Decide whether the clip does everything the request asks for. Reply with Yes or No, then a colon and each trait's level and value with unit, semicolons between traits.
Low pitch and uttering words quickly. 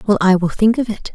No: high, 205 Hz; fast, 315 wpm